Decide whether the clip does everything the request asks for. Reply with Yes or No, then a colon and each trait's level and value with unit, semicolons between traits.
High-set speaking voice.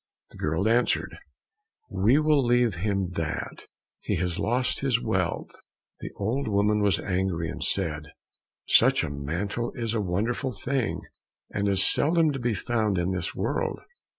No: low, 105 Hz